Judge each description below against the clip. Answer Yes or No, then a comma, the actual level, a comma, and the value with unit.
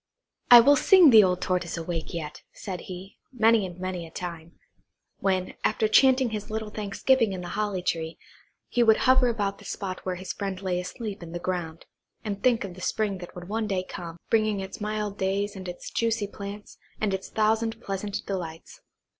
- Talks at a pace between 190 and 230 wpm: Yes, average, 195 wpm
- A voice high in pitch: Yes, high, 195 Hz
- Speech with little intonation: No, average, 3.2 semitones